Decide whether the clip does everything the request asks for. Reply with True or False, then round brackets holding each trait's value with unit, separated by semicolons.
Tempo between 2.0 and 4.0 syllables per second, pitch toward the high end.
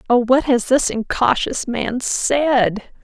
True (3.3 syllables/s; 245 Hz)